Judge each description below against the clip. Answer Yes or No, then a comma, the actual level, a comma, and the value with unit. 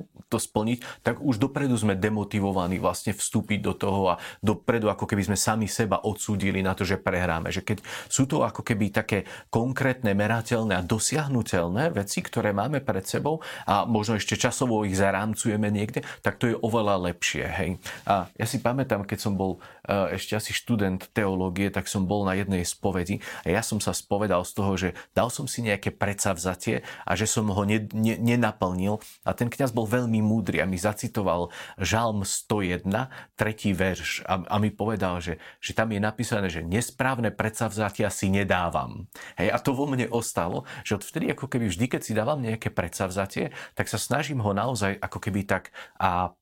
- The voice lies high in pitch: No, low, 105 Hz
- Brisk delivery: Yes, fast, 185 wpm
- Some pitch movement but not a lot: Yes, average, 3.1 semitones